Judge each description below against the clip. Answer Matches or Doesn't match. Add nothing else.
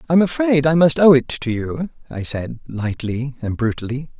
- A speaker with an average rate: Matches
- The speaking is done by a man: Matches